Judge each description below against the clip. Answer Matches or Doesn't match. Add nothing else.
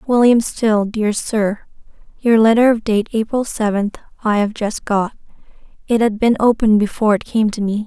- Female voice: Matches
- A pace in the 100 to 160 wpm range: Doesn't match